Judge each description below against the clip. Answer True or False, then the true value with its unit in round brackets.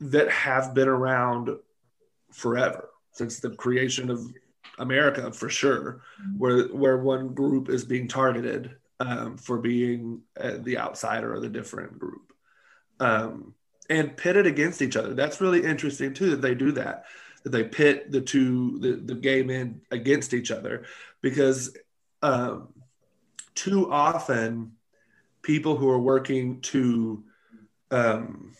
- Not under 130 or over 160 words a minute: True (140 wpm)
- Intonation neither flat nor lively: False (2.3 semitones)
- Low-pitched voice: True (130 Hz)